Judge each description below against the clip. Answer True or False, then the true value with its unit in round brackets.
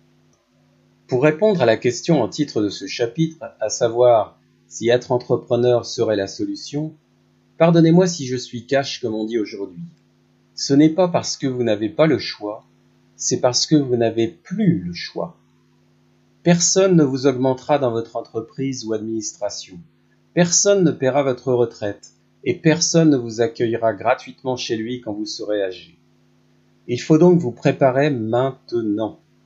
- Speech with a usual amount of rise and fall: False (6.2 semitones)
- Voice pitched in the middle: False (120 Hz)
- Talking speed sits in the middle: True (155 wpm)